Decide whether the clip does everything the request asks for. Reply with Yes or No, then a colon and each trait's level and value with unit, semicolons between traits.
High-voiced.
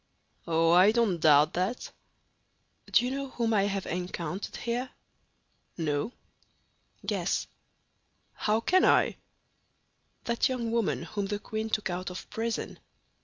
Yes: high, 205 Hz